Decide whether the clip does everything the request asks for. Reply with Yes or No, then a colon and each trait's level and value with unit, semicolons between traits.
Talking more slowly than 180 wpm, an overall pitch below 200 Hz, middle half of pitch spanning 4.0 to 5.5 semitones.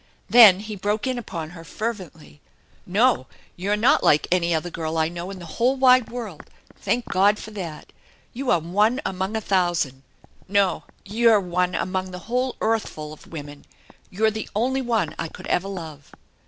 No: average, 185 wpm; high, 190 Hz; average, 4.6 semitones